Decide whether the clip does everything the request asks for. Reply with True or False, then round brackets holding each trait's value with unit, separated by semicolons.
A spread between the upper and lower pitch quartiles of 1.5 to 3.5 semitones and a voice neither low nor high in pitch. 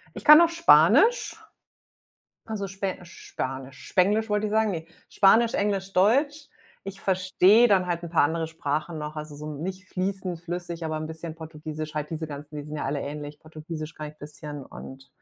False (4.4 semitones; 170 Hz)